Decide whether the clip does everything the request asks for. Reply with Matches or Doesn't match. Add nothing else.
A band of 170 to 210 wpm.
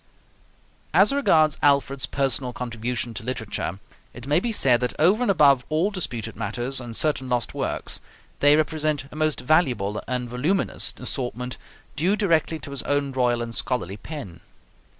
Doesn't match